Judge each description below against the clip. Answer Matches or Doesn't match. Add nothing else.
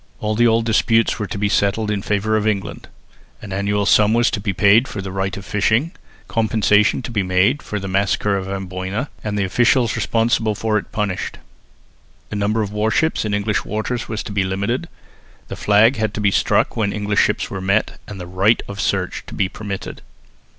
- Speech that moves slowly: Doesn't match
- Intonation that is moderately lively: Doesn't match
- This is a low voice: Matches